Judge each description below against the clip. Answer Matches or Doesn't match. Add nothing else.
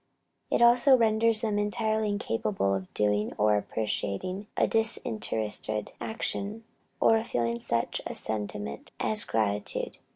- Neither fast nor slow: Doesn't match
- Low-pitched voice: Matches